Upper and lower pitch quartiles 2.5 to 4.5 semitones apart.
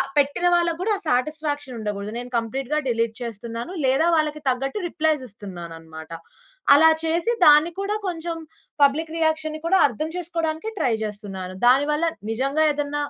No: wide, 5.6 semitones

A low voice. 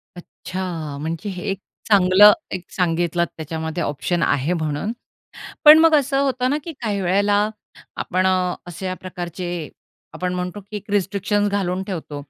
No: medium, 185 Hz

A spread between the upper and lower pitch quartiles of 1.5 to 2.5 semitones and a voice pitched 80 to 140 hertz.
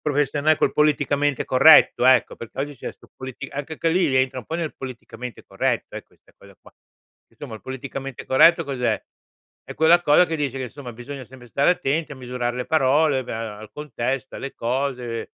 No: average, 2.9 semitones; low, 135 Hz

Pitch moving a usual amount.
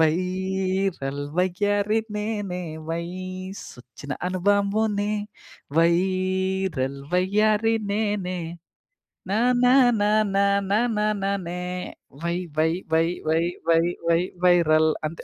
Yes: average, 3.1 semitones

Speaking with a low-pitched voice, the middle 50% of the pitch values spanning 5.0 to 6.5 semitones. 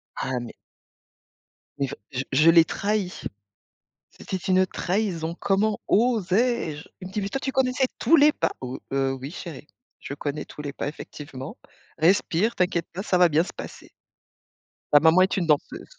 No: medium, 175 Hz; wide, 5.4 semitones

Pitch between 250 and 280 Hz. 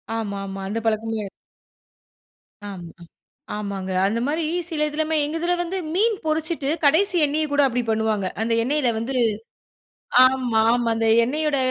Yes: very high, 255 Hz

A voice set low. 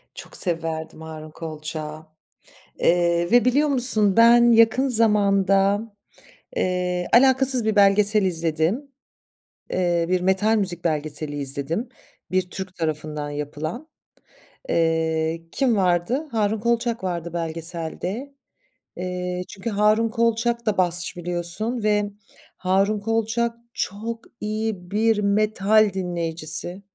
No: high, 190 Hz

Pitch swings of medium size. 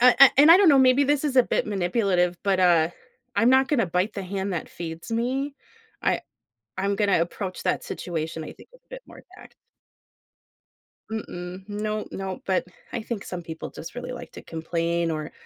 No: wide, 6.1 semitones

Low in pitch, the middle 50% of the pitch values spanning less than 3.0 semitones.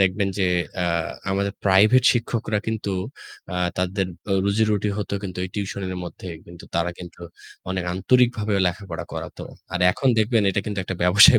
Yes: low, 100 Hz; narrow, 2.6 semitones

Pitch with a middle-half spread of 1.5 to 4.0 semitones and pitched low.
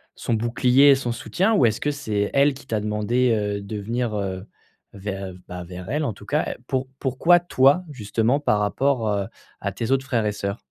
No: average, 4.7 semitones; low, 115 Hz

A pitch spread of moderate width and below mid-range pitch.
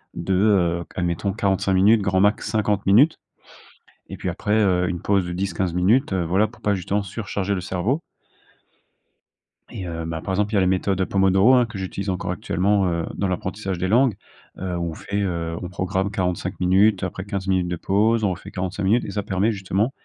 No: narrow, 2.1 semitones; very low, 95 Hz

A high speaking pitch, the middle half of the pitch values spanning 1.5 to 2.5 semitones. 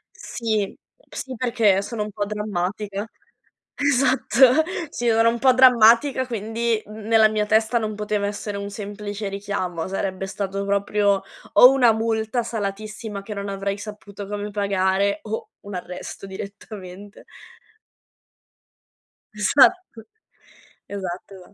Yes: high, 210 Hz; narrow, 2.2 semitones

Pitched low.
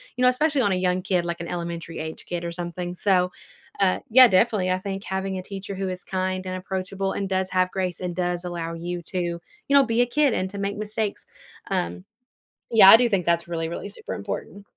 No: medium, 185 Hz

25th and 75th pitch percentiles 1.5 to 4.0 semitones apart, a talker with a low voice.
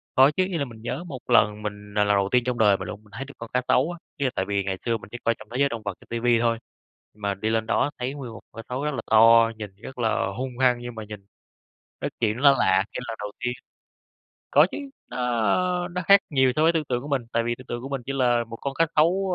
Yes: average, 3.6 semitones; low, 120 Hz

